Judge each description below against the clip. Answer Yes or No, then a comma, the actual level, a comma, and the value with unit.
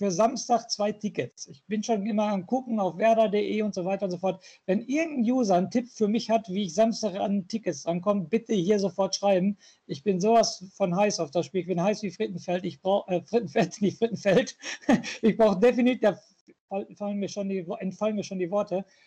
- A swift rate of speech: Yes, fast, 200 wpm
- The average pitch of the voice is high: Yes, high, 205 Hz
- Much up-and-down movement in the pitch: No, average, 2.8 semitones